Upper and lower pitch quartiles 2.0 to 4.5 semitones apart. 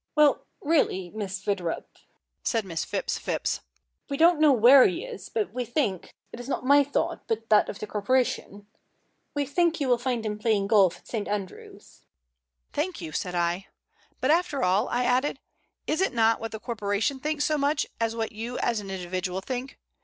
No: wide, 5.6 semitones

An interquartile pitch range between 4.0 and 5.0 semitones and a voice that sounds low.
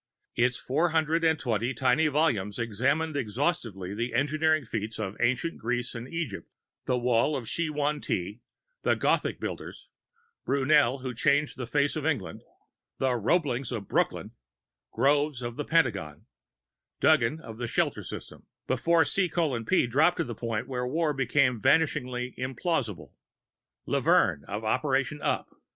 Yes: average, 4.6 semitones; low, 130 Hz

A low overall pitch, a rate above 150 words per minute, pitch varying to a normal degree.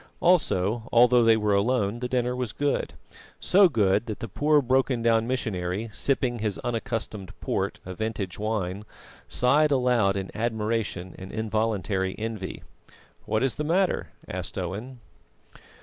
No: low, 115 Hz; average, 140 wpm; average, 3.6 semitones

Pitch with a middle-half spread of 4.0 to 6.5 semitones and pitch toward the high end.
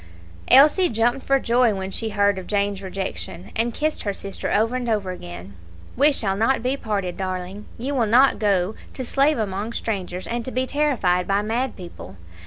Yes: average, 4.7 semitones; high, 215 Hz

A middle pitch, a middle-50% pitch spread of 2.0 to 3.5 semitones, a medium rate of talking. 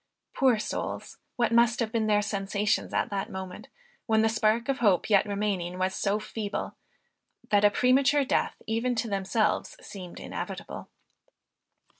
No: high, 215 Hz; narrow, 2.6 semitones; average, 150 wpm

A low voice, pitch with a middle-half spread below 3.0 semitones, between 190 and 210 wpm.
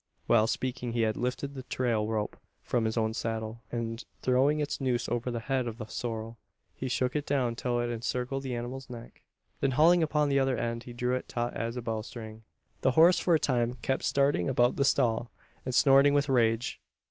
Yes: low, 125 Hz; narrow, 2.5 semitones; fast, 205 wpm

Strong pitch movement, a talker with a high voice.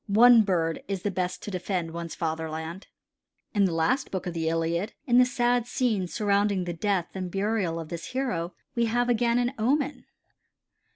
Yes: wide, 5.9 semitones; high, 195 Hz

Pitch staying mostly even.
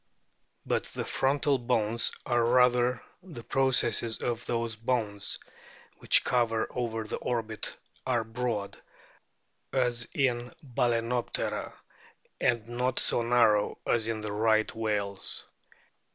Yes: narrow, 1.9 semitones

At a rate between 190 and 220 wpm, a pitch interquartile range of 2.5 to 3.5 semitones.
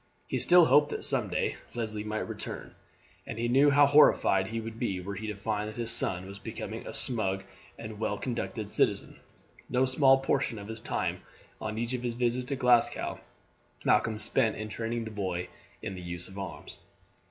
Yes: average, 195 wpm; average, 3.2 semitones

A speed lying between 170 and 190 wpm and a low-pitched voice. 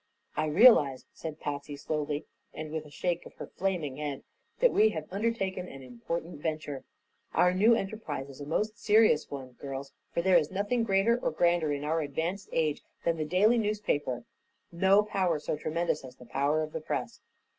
No: average, 185 wpm; medium, 160 Hz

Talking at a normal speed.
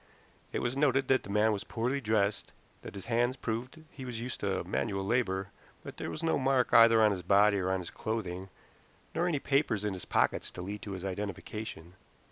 No: fast, 210 wpm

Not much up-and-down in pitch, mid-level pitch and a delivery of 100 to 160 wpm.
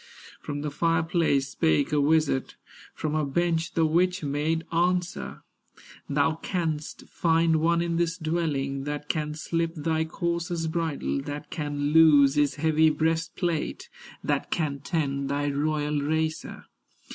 Yes: narrow, 2.2 semitones; medium, 155 Hz; slow, 135 wpm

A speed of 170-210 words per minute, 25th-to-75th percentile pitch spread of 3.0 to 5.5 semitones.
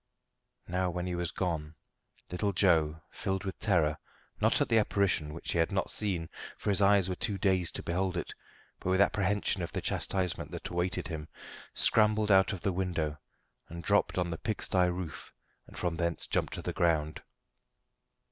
No: average, 180 wpm; narrow, 2.5 semitones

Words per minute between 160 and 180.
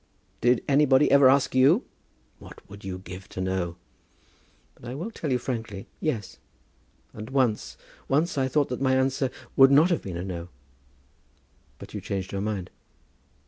Yes: average, 165 wpm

